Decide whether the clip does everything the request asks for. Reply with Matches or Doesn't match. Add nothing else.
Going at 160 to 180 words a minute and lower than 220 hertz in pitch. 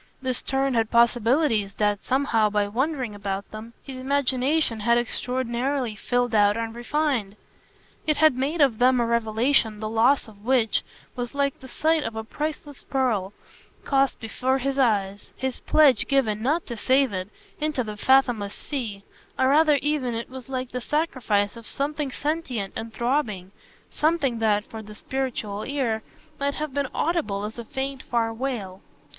Doesn't match